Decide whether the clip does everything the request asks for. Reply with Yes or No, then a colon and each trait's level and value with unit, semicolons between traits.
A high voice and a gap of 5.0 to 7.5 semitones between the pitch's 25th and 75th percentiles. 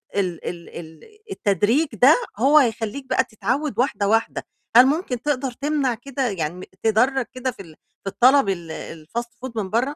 Yes: high, 235 Hz; average, 5.3 semitones